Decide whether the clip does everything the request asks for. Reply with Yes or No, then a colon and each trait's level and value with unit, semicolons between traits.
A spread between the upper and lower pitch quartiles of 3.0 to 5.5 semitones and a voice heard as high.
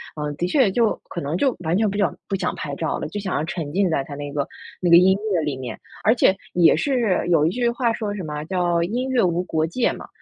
No: average, 5.0 semitones; medium, 180 Hz